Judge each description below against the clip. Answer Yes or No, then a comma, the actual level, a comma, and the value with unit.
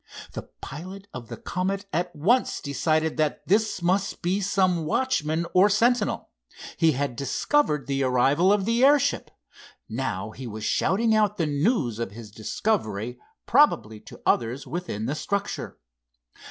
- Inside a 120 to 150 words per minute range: Yes, average, 145 wpm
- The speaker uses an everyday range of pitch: No, wide, 7.4 semitones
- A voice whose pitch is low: No, medium, 165 Hz